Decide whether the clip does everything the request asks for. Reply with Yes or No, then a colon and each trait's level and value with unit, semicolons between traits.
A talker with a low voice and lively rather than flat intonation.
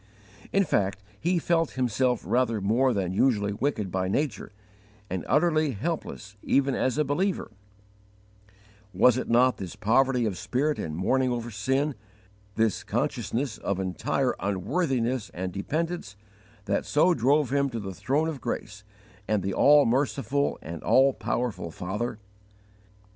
Yes: low, 125 Hz; wide, 5.8 semitones